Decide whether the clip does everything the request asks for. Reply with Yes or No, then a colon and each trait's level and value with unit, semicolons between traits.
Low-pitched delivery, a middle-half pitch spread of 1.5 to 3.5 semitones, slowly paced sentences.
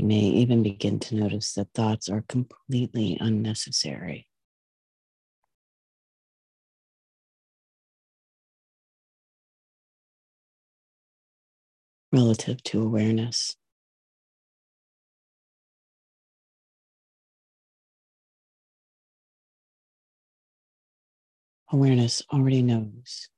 Yes: low, 110 Hz; narrow, 2.5 semitones; slow, 40 wpm